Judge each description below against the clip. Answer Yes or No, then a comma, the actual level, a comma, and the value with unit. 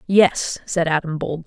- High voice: No, medium, 170 Hz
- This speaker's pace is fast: No, average, 165 wpm